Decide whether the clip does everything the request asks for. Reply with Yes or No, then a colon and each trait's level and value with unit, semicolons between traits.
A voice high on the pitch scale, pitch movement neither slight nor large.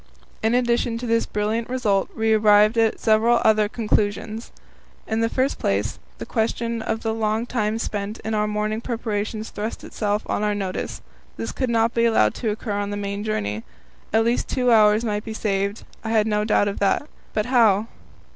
No: high, 220 Hz; narrow, 1.7 semitones